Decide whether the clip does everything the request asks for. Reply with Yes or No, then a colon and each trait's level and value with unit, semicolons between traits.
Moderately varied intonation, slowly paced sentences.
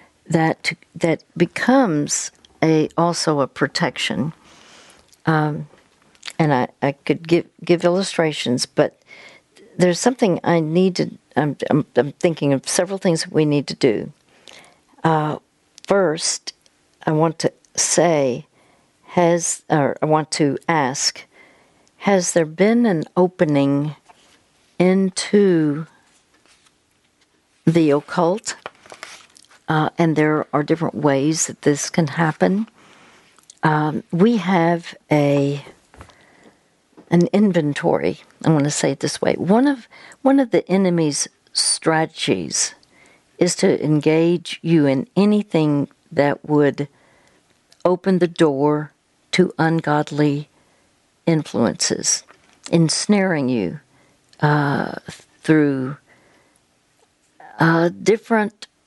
Yes: average, 3.3 semitones; slow, 105 wpm